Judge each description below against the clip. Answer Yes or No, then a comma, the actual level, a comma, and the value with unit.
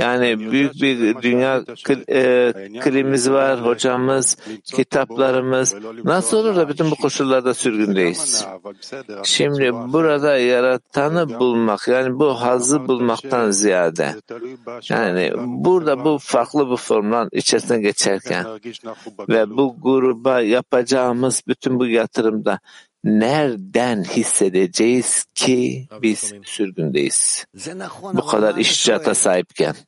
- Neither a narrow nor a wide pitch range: Yes, average, 3.3 semitones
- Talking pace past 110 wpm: No, average, 100 wpm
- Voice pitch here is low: Yes, low, 125 Hz